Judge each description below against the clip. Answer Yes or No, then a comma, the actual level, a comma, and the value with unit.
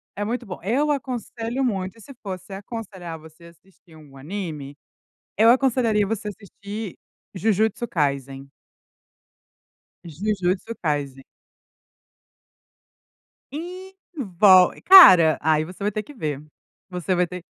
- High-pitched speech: Yes, high, 195 Hz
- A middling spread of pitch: No, wide, 5.7 semitones